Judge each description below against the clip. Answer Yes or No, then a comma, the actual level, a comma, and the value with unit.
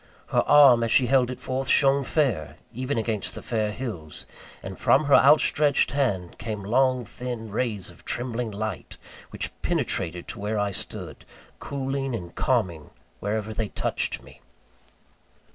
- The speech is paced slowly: No, average, 150 wpm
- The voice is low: Yes, low, 115 Hz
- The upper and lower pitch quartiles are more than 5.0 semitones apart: No, average, 4.3 semitones